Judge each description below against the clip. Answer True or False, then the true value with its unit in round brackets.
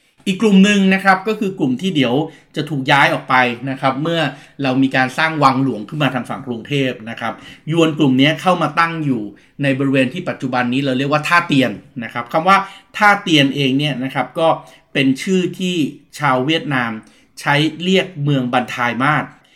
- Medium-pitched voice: True (145 Hz)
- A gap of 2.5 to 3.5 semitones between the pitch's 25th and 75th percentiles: False (4.2 semitones)